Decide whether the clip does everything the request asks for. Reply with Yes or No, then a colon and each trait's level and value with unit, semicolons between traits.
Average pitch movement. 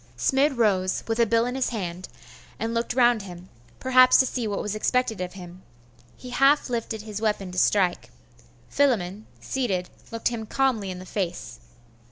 Yes: average, 4.9 semitones